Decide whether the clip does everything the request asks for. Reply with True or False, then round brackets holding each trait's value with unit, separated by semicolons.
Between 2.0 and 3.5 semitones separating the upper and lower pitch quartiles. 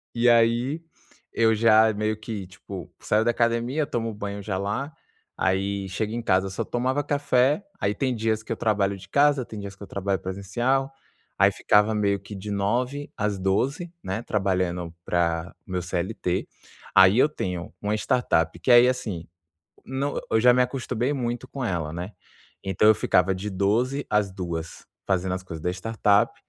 False (4.2 semitones)